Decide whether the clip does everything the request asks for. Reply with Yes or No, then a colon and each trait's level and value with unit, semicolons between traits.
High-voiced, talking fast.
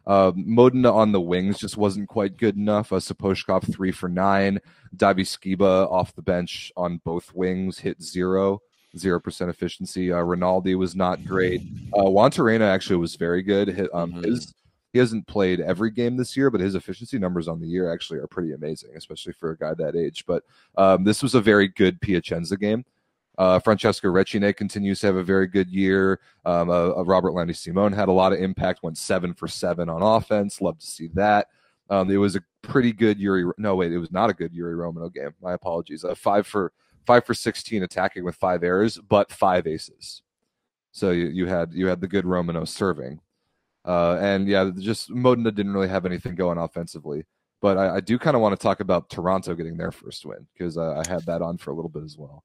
No: very low, 95 Hz; fast, 210 wpm